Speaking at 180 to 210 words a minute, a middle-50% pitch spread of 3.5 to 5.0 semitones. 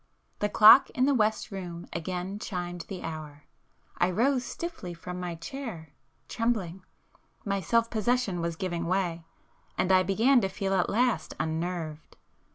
No: average, 145 wpm; average, 4.4 semitones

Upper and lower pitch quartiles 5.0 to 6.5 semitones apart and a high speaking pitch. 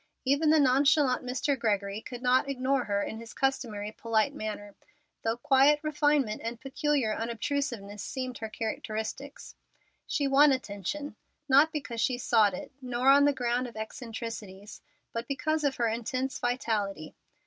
No: average, 4.1 semitones; very high, 250 Hz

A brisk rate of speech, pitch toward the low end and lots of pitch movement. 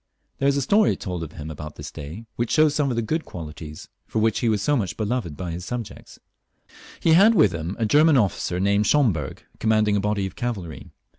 Yes: fast, 215 wpm; low, 105 Hz; wide, 6.5 semitones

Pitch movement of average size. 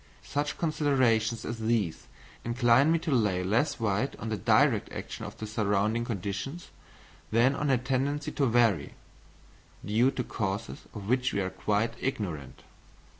Yes: average, 4.3 semitones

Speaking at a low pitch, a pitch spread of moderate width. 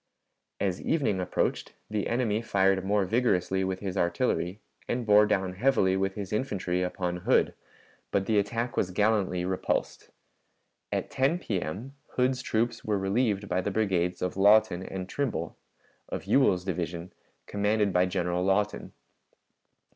Yes: low, 100 Hz; average, 3.1 semitones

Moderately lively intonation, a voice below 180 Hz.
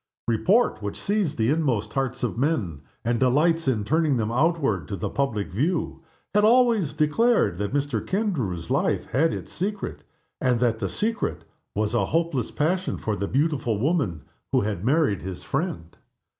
No: wide, 7.5 semitones; low, 135 Hz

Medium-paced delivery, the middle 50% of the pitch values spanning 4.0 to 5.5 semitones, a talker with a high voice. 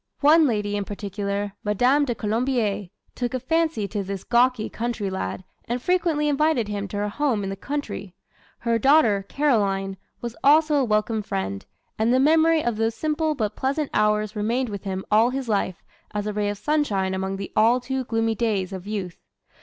Yes: average, 185 wpm; average, 4.8 semitones; high, 220 Hz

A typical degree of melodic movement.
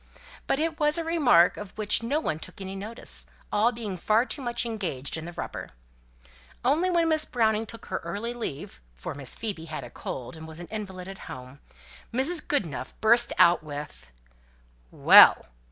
No: wide, 6.9 semitones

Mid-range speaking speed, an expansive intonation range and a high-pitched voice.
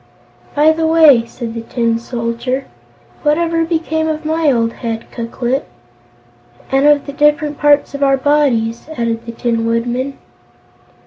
No: average, 150 wpm; average, 4.3 semitones; very high, 270 Hz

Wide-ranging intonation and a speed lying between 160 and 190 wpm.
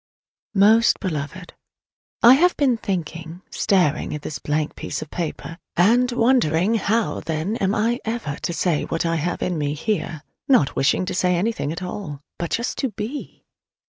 Yes: wide, 6.0 semitones; average, 170 wpm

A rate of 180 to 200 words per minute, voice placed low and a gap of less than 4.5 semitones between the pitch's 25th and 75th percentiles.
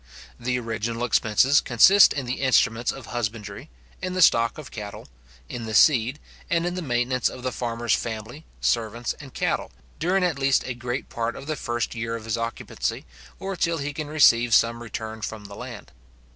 Yes: average, 185 wpm; low, 120 Hz; average, 3.5 semitones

